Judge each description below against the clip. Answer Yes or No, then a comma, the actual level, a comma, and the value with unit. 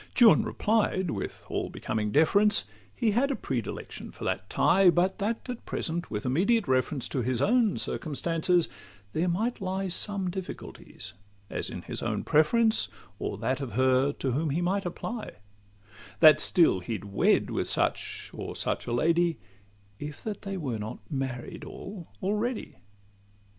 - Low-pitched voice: No, medium, 175 Hz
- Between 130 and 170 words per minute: Yes, average, 155 wpm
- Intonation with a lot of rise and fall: Yes, wide, 7.1 semitones